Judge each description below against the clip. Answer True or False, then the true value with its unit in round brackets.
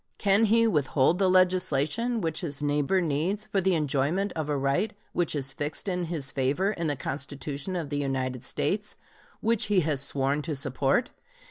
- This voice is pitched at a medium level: True (155 Hz)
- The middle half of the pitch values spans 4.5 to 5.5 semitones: True (5.2 semitones)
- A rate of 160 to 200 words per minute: True (175 wpm)